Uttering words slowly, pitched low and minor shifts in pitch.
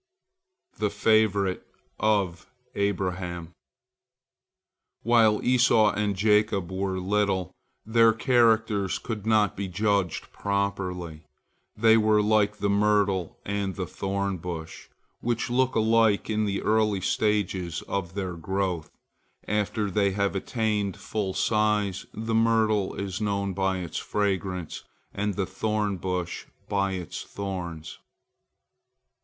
Yes: slow, 115 wpm; low, 100 Hz; narrow, 2.3 semitones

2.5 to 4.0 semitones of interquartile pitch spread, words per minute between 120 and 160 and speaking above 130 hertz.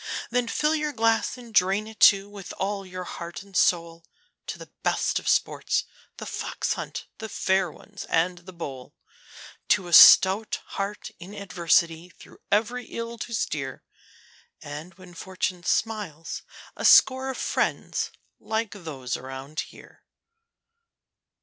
No: average, 4.5 semitones; average, 145 wpm; high, 190 Hz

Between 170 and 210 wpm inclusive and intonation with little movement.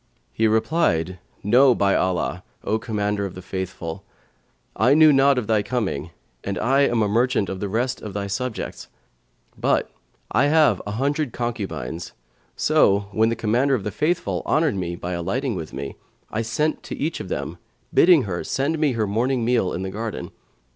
No: average, 180 wpm; average, 5.3 semitones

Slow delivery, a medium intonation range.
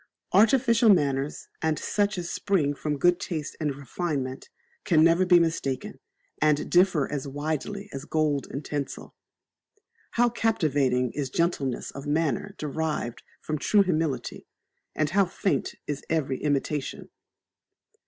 Yes: slow, 130 wpm; average, 4.0 semitones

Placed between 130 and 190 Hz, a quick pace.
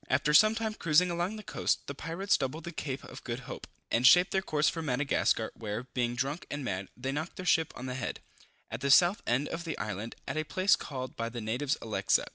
Yes: medium, 140 Hz; fast, 235 wpm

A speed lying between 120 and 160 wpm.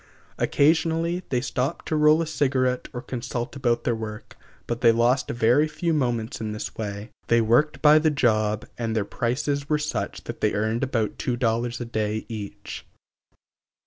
No: average, 175 wpm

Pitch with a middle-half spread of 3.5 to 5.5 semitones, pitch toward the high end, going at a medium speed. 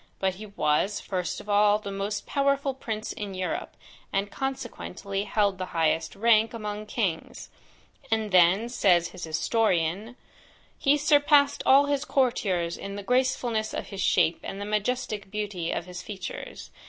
Yes: average, 3.9 semitones; high, 205 Hz; average, 155 wpm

